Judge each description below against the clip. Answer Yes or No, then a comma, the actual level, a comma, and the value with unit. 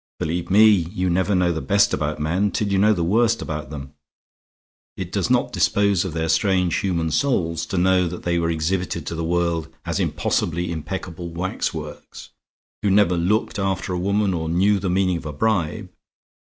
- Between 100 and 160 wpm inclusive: No, average, 190 wpm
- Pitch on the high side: No, very low, 90 Hz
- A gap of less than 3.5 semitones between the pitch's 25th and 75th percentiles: Yes, average, 2.8 semitones